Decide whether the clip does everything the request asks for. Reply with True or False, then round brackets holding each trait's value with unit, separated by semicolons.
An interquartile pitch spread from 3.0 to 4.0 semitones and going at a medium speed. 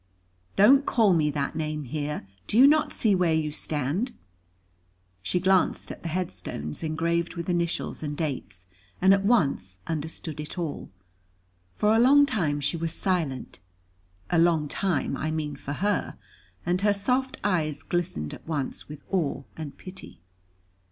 False (4.4 semitones; 155 wpm)